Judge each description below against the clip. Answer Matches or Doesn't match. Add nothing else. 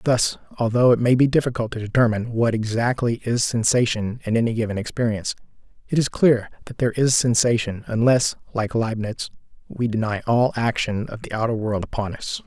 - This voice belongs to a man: Matches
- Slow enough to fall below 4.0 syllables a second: Doesn't match